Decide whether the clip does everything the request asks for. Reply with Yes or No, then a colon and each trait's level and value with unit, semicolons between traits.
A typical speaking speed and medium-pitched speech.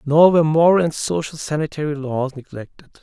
Yes: average, 160 wpm; medium, 150 Hz